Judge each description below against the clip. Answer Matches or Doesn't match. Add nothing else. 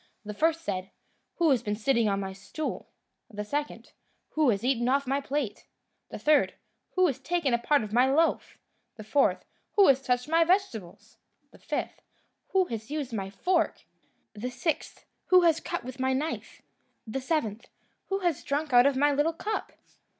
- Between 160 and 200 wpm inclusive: Matches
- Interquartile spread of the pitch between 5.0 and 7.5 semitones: Matches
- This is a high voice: Matches